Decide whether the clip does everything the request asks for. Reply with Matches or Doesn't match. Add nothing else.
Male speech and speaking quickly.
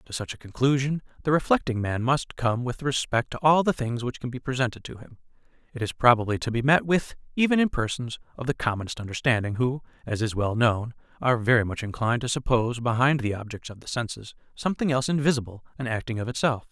Matches